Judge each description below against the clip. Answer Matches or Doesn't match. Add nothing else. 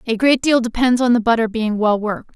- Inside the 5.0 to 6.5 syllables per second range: Matches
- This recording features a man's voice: Doesn't match